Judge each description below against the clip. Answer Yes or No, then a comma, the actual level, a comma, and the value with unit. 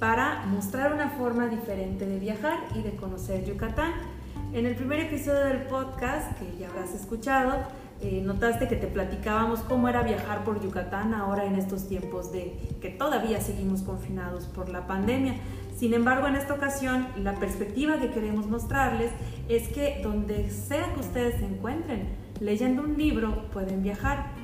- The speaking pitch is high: Yes, high, 215 Hz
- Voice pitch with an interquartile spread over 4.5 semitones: Yes, average, 5.3 semitones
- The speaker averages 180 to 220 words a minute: No, average, 160 wpm